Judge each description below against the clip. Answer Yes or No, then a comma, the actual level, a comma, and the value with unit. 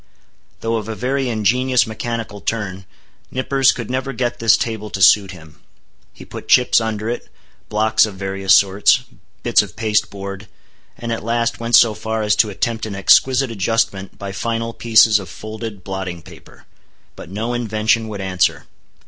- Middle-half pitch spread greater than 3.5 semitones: No, average, 2.8 semitones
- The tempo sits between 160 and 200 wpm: Yes, average, 165 wpm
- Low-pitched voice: Yes, low, 110 Hz